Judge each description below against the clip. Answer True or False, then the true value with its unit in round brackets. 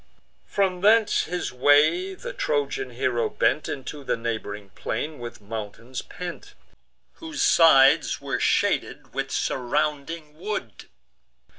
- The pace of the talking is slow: True (115 wpm)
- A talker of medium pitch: True (155 Hz)